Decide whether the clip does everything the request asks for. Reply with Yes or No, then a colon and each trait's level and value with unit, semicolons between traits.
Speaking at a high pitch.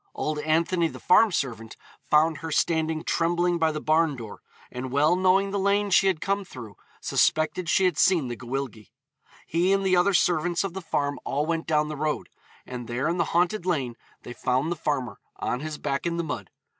No: medium, 160 Hz